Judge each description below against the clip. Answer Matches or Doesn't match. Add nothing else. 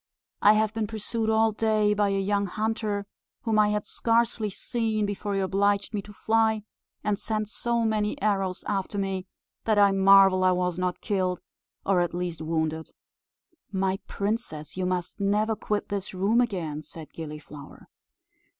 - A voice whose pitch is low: Doesn't match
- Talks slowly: Doesn't match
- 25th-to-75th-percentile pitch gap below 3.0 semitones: Matches